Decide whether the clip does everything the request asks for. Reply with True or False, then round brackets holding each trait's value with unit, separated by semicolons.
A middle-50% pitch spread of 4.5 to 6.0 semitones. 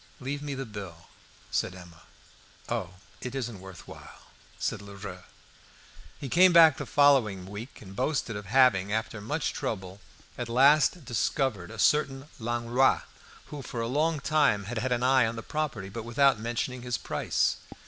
True (5.0 semitones)